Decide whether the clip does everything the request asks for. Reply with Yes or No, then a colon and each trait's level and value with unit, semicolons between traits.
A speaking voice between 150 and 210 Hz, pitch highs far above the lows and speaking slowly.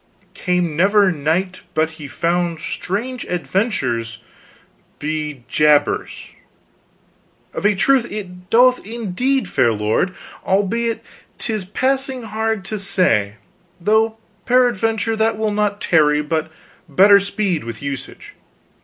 Yes: high, 190 Hz; wide, 6.0 semitones; slow, 110 wpm